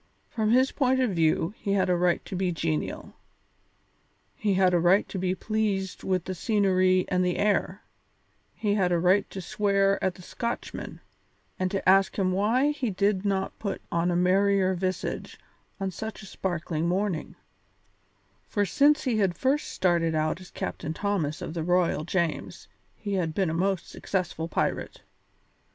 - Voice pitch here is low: No, high, 190 Hz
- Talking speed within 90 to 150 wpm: No, average, 170 wpm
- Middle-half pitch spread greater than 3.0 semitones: No, narrow, 2.4 semitones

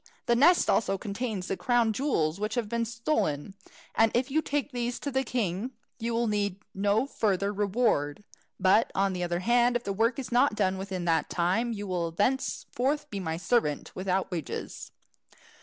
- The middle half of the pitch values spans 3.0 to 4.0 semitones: No, average, 4.4 semitones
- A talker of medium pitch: No, high, 210 Hz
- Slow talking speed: No, average, 180 wpm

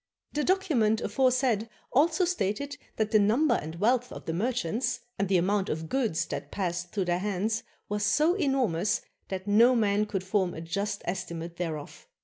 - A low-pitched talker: No, high, 210 Hz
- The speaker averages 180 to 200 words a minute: No, average, 170 wpm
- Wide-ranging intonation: Yes, wide, 5.7 semitones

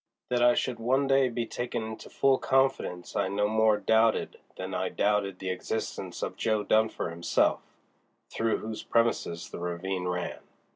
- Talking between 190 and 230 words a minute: No, average, 160 wpm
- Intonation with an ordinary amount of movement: Yes, average, 4.1 semitones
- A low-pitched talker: Yes, low, 110 Hz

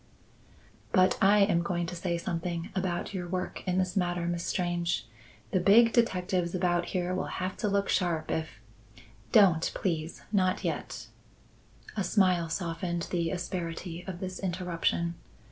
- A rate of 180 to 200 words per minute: No, average, 150 wpm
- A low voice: No, medium, 180 Hz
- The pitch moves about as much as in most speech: No, narrow, 1.6 semitones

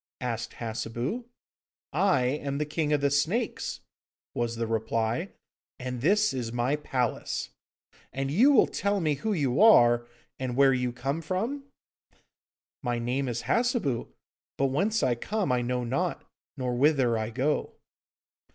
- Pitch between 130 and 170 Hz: Yes, low, 135 Hz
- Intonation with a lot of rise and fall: Yes, wide, 5.7 semitones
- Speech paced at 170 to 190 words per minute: No, average, 145 wpm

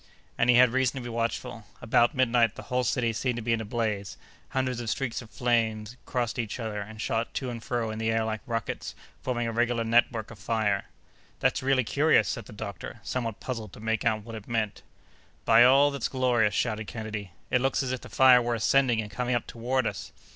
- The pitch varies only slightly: Yes, narrow, 2.1 semitones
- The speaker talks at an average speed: No, fast, 220 wpm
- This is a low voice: Yes, low, 115 Hz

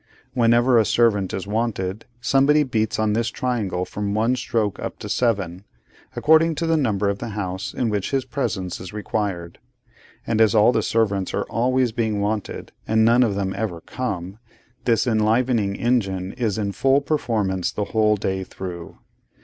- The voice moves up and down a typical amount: Yes, average, 3.3 semitones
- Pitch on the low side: Yes, low, 110 Hz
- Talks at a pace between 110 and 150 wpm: No, average, 170 wpm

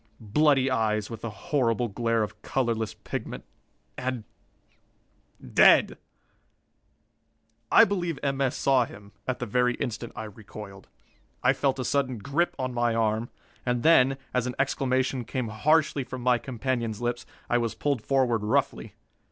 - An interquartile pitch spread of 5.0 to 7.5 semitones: No, average, 3.1 semitones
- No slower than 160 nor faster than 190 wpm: No, average, 145 wpm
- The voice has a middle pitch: No, low, 125 Hz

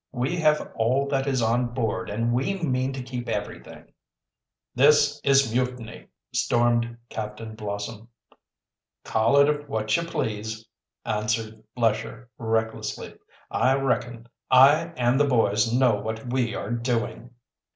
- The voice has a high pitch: No, low, 120 Hz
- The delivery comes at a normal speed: No, slow, 130 wpm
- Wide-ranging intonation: No, average, 3.2 semitones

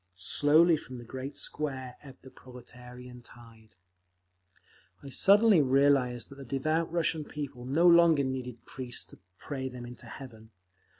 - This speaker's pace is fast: No, average, 140 wpm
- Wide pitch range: No, average, 3.3 semitones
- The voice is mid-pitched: No, low, 130 Hz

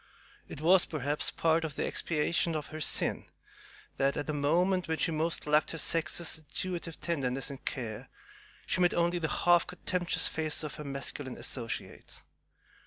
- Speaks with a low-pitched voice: No, medium, 155 Hz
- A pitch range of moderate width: Yes, average, 3.0 semitones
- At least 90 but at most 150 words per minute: No, average, 165 wpm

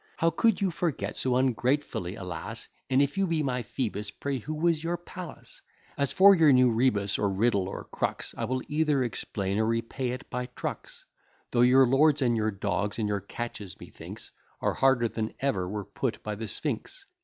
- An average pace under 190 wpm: No, average, 195 wpm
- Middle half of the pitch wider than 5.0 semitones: Yes, wide, 5.6 semitones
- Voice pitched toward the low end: Yes, low, 125 Hz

